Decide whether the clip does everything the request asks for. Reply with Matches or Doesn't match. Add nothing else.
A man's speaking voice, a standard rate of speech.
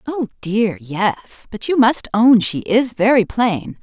Doesn't match